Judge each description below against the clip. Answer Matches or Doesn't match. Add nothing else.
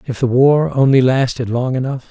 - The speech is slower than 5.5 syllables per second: Matches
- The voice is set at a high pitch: Doesn't match